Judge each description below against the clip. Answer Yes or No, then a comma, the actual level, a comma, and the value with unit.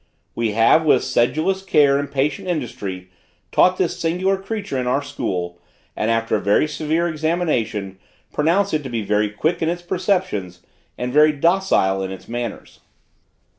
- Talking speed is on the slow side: No, average, 160 wpm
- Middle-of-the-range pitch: Yes, medium, 145 Hz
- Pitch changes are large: Yes, wide, 7.7 semitones